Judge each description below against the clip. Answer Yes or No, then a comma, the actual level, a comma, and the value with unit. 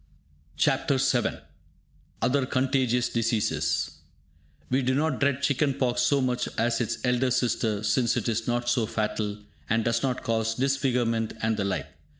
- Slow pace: No, average, 155 wpm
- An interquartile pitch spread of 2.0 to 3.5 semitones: Yes, narrow, 2.4 semitones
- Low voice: Yes, low, 120 Hz